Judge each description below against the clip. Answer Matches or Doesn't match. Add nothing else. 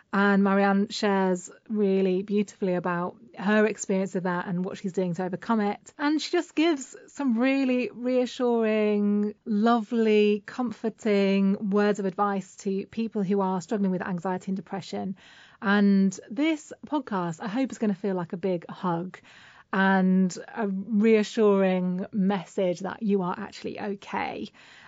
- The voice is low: Doesn't match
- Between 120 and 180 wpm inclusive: Matches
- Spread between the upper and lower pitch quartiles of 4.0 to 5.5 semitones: Doesn't match